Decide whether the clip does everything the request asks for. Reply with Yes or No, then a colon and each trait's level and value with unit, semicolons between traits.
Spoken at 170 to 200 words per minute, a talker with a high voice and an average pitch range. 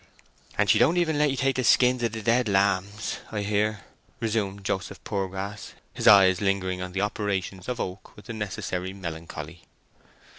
No: average, 175 wpm; low, 100 Hz; average, 3.1 semitones